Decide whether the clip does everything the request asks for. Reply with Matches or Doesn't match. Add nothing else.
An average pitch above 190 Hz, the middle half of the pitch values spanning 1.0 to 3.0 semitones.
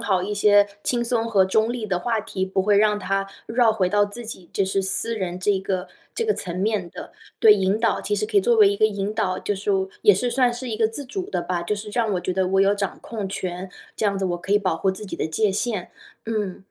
Matches